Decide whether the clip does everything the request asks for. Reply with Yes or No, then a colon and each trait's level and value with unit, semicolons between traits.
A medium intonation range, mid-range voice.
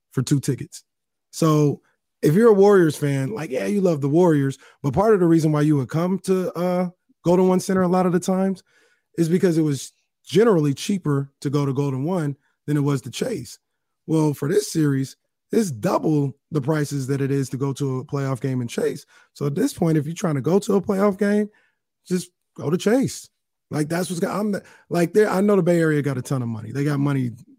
Yes: average, 4.8 semitones; medium, 160 Hz